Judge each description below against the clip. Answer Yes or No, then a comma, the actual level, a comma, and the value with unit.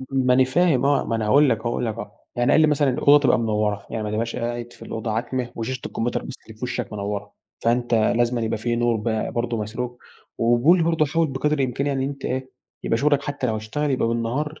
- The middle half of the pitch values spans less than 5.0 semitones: Yes, average, 3.2 semitones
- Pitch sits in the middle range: No, low, 120 Hz